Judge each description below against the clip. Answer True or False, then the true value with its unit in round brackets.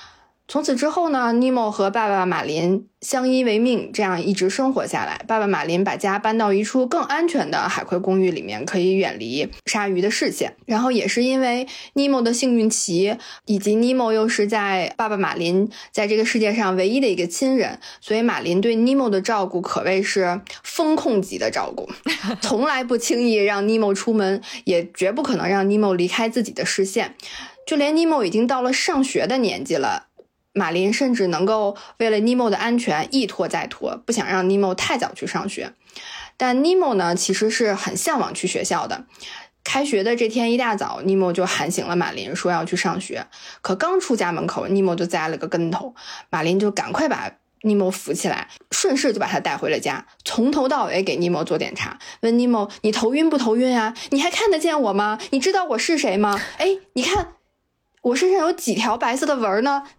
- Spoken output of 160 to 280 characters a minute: False (290 characters per minute)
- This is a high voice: True (220 Hz)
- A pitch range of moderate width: True (5.0 semitones)